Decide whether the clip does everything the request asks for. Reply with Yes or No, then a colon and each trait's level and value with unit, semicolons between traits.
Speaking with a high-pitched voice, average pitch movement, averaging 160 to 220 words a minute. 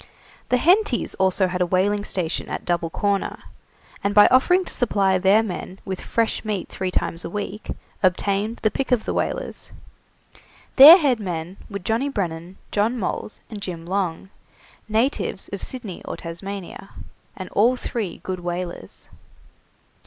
No: high, 200 Hz; average, 3.6 semitones; average, 150 wpm